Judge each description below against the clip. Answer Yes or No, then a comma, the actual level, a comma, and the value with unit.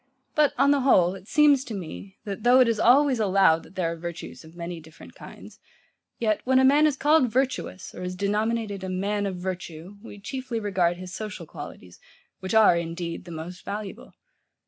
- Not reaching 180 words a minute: No, average, 195 wpm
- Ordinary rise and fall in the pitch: No, wide, 5.7 semitones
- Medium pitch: No, high, 200 Hz